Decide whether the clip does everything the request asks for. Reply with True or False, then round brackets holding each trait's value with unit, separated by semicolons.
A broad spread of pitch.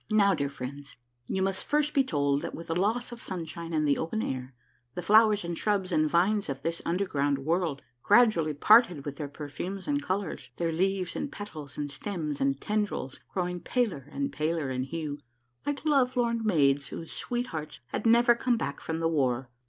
True (6.6 semitones)